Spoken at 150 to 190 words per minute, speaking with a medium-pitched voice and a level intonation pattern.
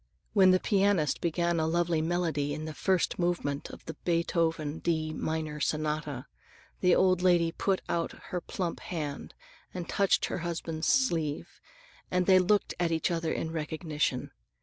Yes: average, 155 wpm; medium, 165 Hz; narrow, 2.3 semitones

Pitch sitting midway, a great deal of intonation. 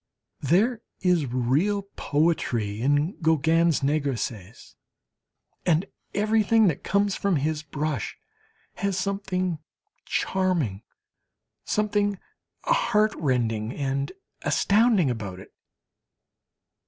Yes: medium, 160 Hz; wide, 6.7 semitones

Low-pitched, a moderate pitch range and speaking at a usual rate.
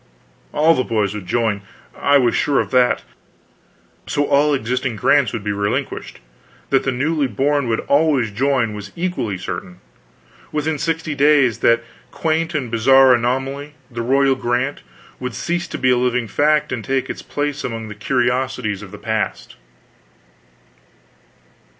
Yes: low, 130 Hz; average, 4.0 semitones; average, 150 wpm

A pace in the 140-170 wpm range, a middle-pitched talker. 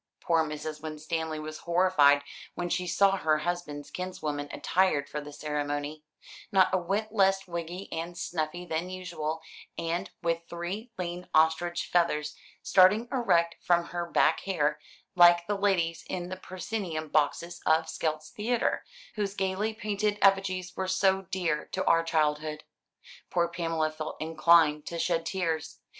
Yes: average, 145 wpm; medium, 170 Hz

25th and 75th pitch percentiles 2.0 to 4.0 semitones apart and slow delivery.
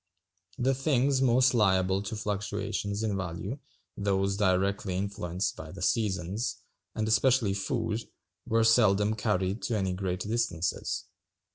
Yes: average, 3.1 semitones; slow, 125 wpm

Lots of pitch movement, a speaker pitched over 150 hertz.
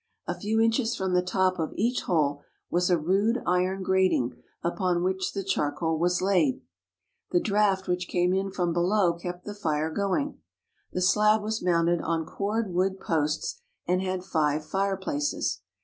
No: average, 2.7 semitones; medium, 185 Hz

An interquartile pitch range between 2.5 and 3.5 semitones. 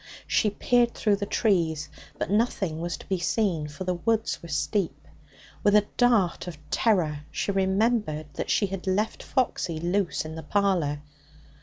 No: average, 4.4 semitones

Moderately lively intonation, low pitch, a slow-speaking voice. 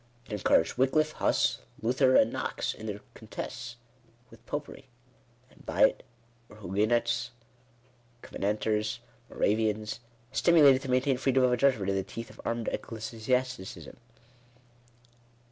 Yes: average, 3.3 semitones; low, 115 Hz; slow, 125 wpm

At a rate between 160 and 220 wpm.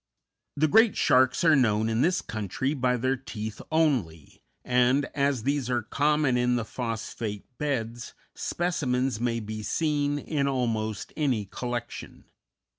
No: average, 140 wpm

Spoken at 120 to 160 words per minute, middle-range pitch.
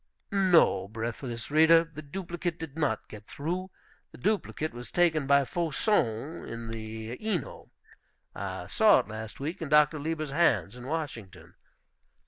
Yes: average, 140 wpm; medium, 145 Hz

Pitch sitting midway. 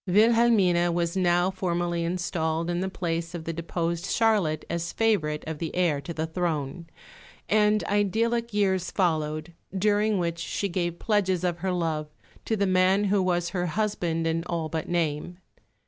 Yes: medium, 175 Hz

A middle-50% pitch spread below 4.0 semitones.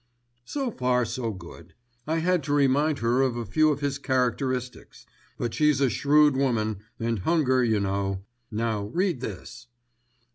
No: average, 4.3 semitones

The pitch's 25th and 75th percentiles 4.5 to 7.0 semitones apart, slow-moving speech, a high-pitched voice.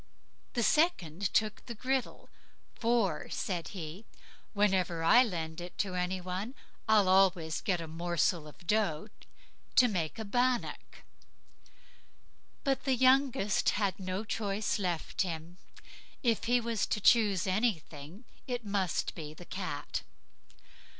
Yes: average, 4.8 semitones; slow, 130 wpm; high, 195 Hz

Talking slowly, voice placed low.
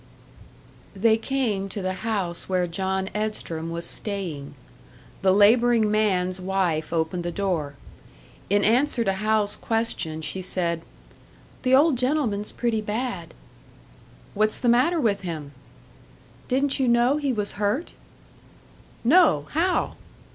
No: slow, 125 wpm; high, 205 Hz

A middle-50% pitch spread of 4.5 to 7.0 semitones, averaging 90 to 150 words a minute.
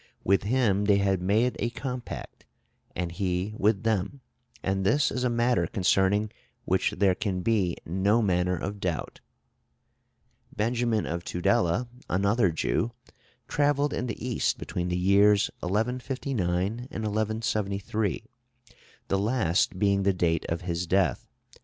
No: average, 3.9 semitones; slow, 135 wpm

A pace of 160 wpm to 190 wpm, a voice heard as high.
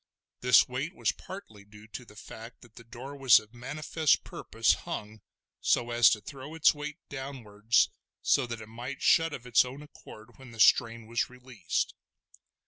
No: average, 175 wpm; low, 120 Hz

